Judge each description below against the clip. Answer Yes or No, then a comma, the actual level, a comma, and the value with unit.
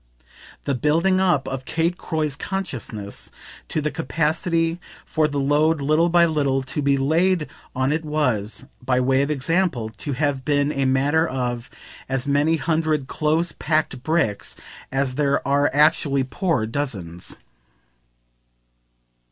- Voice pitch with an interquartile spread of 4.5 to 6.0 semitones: No, average, 3.3 semitones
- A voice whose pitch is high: No, medium, 145 Hz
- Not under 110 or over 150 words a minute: Yes, slow, 135 wpm